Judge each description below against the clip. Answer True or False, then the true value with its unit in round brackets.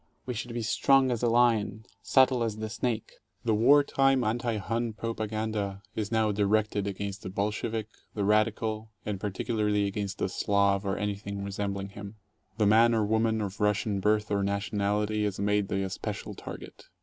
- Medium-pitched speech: False (105 Hz)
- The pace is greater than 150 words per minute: True (175 wpm)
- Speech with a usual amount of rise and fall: False (1.9 semitones)